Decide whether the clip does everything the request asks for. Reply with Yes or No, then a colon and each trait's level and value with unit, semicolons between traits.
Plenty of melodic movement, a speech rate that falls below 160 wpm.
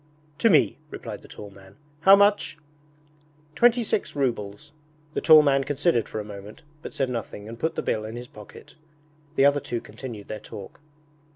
No: wide, 6.4 semitones; average, 180 wpm